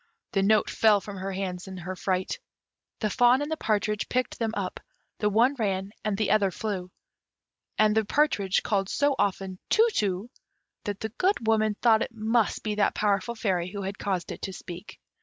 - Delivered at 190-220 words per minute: Yes, average, 195 wpm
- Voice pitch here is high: Yes, high, 210 Hz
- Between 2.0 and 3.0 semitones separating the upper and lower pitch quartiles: Yes, narrow, 2.6 semitones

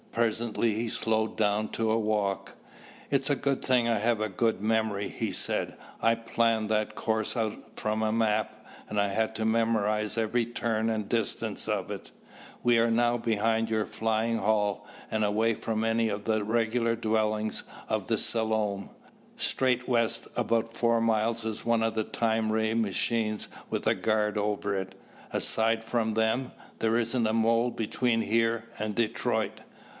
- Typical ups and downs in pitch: No, narrow, 1.1 semitones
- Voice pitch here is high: No, low, 110 Hz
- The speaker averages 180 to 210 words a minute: No, average, 165 wpm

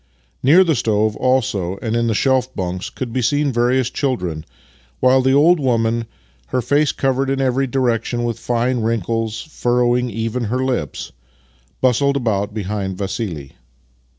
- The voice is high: No, low, 120 Hz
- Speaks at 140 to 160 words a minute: Yes, average, 150 wpm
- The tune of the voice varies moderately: Yes, average, 3.6 semitones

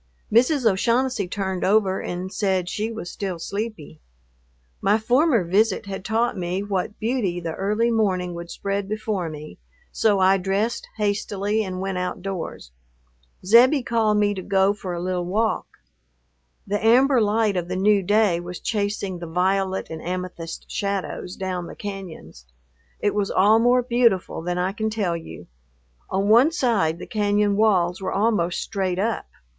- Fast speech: No, average, 160 wpm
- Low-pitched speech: No, high, 200 Hz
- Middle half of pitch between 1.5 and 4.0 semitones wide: Yes, average, 3.1 semitones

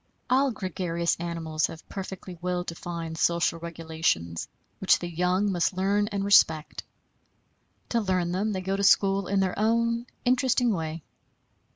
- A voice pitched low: No, medium, 185 Hz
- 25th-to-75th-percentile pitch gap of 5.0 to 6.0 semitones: No, average, 3.2 semitones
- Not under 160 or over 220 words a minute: No, average, 145 wpm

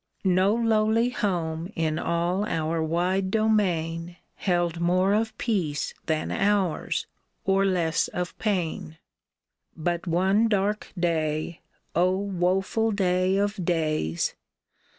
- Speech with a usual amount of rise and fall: Yes, average, 3.3 semitones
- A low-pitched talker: No, medium, 180 Hz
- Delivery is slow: Yes, slow, 110 wpm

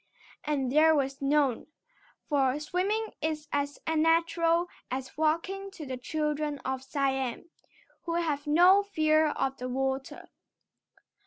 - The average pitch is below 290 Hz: No, very high, 300 Hz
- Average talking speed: No, slow, 125 wpm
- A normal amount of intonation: Yes, average, 3.5 semitones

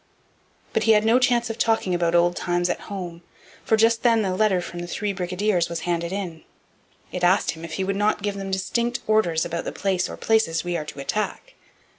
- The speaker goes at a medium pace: No, fast, 220 wpm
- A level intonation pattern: No, average, 3.8 semitones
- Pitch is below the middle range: No, high, 190 Hz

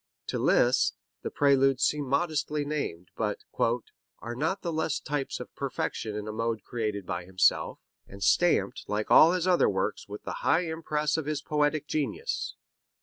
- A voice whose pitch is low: No, medium, 145 Hz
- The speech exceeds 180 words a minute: No, average, 165 wpm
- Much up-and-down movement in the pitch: Yes, wide, 6.4 semitones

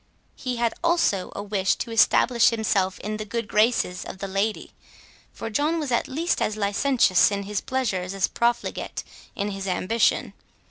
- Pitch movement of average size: Yes, average, 3.4 semitones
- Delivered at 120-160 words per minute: No, average, 170 wpm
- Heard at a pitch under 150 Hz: No, high, 215 Hz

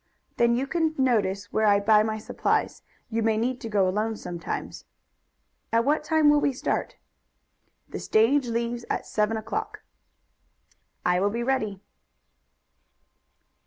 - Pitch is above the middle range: Yes, high, 225 Hz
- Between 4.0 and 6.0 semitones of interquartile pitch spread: No, average, 3.5 semitones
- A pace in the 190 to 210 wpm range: No, average, 140 wpm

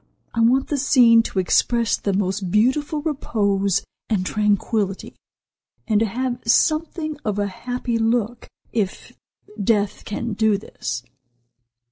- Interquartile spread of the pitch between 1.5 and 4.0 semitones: Yes, average, 3.5 semitones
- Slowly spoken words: Yes, slow, 125 wpm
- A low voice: No, high, 225 Hz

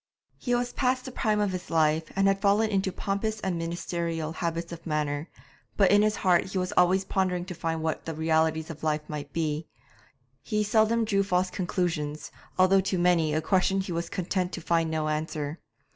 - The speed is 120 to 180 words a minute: No, average, 190 wpm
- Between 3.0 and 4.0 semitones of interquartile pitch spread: Yes, average, 3.5 semitones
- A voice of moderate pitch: Yes, medium, 175 Hz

